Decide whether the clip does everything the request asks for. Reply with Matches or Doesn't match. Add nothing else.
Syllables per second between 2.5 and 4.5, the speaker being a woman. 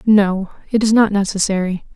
Doesn't match